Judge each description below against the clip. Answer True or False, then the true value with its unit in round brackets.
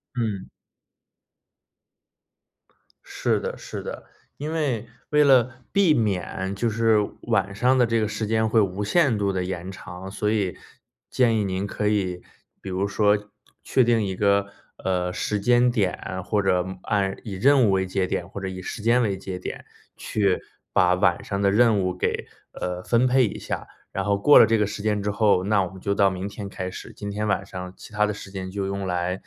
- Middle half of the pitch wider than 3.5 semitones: False (2.8 semitones)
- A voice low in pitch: True (100 Hz)